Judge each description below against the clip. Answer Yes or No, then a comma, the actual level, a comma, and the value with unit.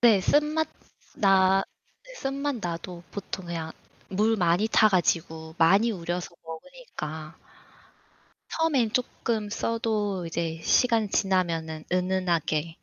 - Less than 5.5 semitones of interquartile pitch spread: Yes, average, 5.1 semitones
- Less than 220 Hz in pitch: Yes, high, 190 Hz